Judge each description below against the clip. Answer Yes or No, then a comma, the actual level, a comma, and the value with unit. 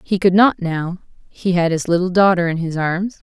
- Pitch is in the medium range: Yes, medium, 180 Hz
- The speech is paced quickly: Yes, fast, 220 wpm